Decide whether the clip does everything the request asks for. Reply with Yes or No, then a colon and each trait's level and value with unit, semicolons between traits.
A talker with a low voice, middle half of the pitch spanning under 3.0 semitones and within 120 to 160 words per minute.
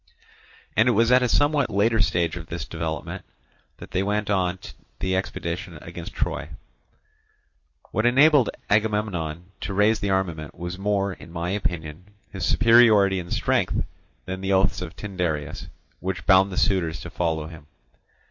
No: very low, 95 Hz; average, 3.5 semitones; average, 155 wpm